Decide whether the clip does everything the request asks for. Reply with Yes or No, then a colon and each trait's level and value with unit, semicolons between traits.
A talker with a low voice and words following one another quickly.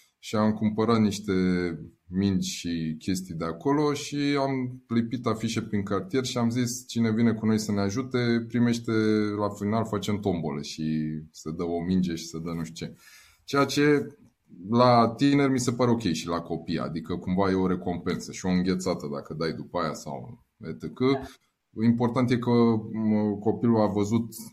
Yes: low, 105 Hz; fast, 175 wpm